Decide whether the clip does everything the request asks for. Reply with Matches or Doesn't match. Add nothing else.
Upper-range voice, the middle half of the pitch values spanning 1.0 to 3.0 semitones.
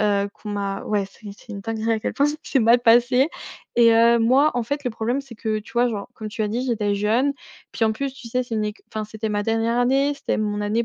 Matches